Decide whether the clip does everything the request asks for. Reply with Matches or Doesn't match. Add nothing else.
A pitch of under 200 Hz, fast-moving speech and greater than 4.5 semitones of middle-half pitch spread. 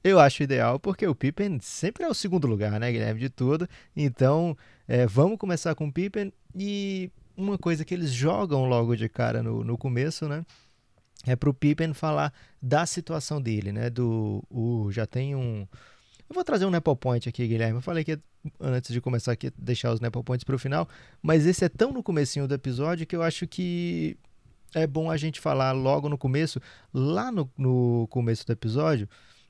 Matches